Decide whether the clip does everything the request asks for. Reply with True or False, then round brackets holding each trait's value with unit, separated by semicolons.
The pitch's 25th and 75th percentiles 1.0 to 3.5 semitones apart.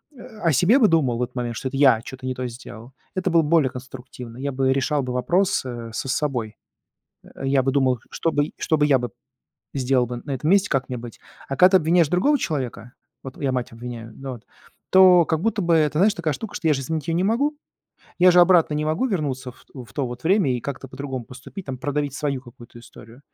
False (4.7 semitones)